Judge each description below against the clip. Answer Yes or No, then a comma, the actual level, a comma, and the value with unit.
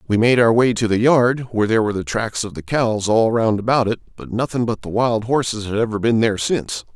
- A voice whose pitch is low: Yes, low, 115 Hz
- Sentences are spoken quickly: Yes, fast, 260 wpm